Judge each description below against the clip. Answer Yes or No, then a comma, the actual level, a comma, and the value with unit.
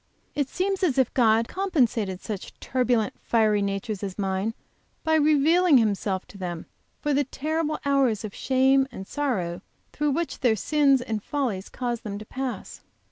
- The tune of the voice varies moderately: No, wide, 5.8 semitones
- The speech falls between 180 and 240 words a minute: No, average, 165 wpm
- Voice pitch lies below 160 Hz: No, high, 245 Hz